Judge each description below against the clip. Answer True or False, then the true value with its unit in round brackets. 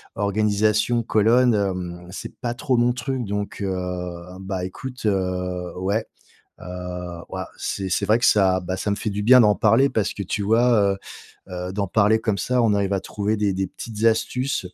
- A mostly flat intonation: False (3.0 semitones)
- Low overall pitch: True (105 Hz)